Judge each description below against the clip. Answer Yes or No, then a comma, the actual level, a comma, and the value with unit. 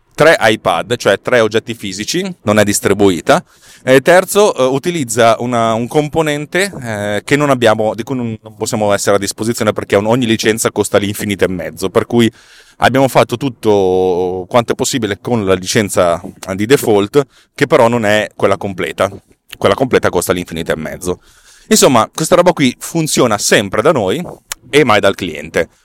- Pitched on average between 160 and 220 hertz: No, low, 115 Hz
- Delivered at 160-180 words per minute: Yes, average, 165 wpm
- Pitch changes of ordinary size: Yes, average, 4.8 semitones